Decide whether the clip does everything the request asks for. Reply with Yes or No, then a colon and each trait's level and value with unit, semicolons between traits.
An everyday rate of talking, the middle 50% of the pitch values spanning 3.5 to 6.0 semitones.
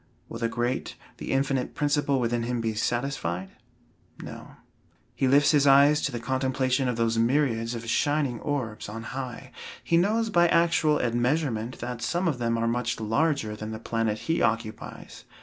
Yes: average, 165 wpm; average, 3.8 semitones